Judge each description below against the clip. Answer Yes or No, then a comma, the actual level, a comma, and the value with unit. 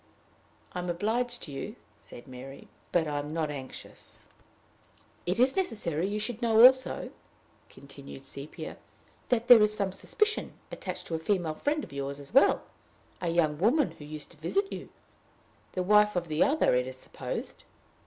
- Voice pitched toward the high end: No, medium, 180 Hz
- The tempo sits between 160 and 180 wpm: Yes, average, 170 wpm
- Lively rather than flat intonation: Yes, wide, 7.6 semitones